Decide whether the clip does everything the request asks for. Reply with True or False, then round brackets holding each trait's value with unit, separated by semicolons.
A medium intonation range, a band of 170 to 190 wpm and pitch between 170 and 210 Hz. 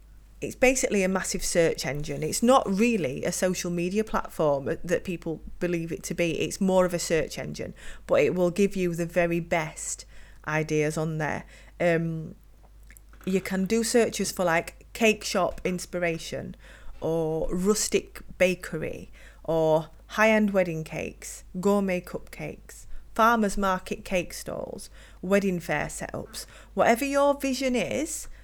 False (4.0 semitones; 140 wpm; 185 Hz)